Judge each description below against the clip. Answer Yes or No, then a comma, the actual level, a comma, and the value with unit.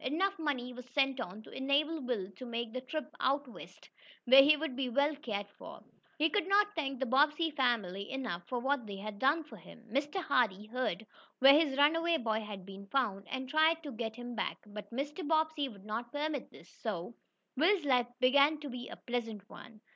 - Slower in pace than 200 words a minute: No, fast, 205 wpm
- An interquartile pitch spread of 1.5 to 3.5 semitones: No, average, 4.7 semitones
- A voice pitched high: Yes, very high, 260 Hz